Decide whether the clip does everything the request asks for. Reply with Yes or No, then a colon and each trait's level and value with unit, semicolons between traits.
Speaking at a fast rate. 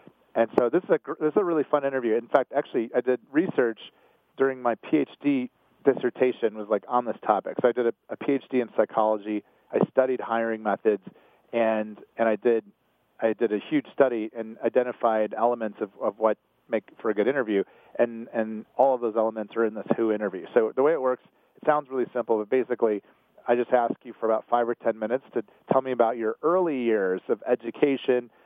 Yes: fast, 210 wpm